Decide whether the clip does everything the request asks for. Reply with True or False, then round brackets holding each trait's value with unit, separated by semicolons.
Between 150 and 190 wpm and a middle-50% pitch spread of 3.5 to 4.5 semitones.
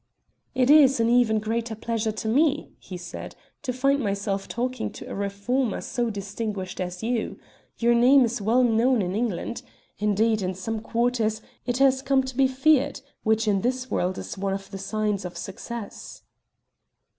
True (170 wpm; 3.8 semitones)